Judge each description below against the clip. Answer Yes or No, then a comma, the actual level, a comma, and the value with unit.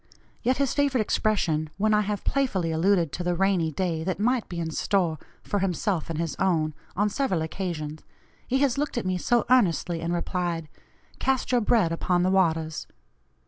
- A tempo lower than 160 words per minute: No, average, 185 wpm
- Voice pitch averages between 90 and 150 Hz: No, medium, 185 Hz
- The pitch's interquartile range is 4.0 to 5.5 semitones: Yes, average, 4.6 semitones